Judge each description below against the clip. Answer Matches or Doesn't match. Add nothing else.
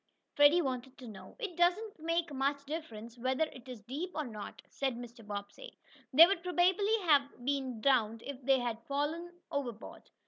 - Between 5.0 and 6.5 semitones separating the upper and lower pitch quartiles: Matches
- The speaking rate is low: Doesn't match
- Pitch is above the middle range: Matches